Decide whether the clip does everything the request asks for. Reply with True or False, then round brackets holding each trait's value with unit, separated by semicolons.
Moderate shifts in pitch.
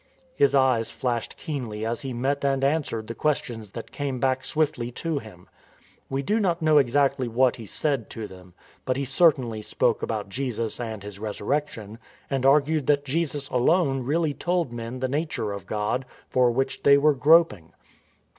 True (4.1 semitones)